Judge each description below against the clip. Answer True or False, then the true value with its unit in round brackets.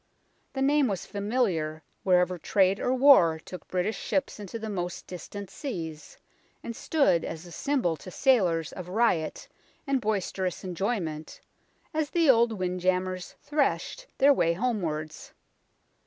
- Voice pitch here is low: False (190 Hz)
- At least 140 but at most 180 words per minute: True (145 wpm)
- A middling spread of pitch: False (6.2 semitones)